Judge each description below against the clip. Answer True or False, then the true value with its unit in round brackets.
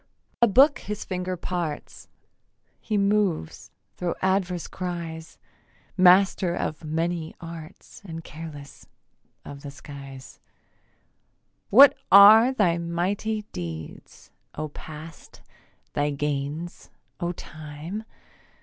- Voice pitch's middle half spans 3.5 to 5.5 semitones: True (4.0 semitones)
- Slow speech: True (95 wpm)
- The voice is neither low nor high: True (170 Hz)